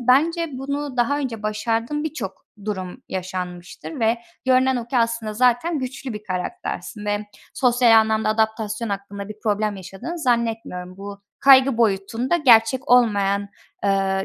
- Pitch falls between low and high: No, high, 225 Hz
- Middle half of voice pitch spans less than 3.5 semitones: No, average, 4.2 semitones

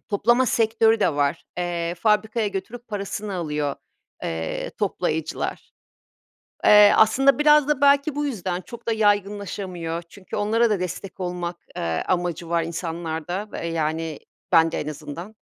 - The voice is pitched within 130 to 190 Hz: Yes, medium, 185 Hz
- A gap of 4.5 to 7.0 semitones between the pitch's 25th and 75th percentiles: Yes, average, 4.8 semitones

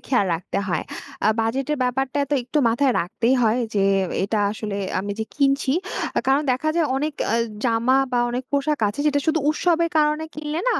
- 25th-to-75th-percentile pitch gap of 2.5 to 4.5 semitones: No, average, 4.9 semitones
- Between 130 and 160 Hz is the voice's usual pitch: No, very high, 265 Hz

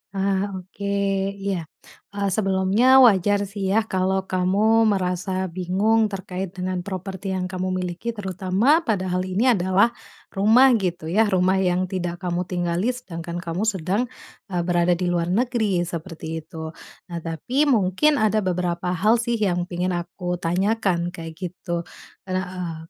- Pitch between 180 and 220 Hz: Yes, medium, 185 Hz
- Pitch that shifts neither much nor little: No, narrow, 2.0 semitones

